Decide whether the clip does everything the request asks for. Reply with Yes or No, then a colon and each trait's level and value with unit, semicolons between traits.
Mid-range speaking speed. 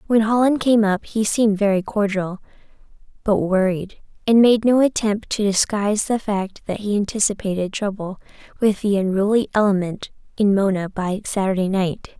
Yes: average, 155 wpm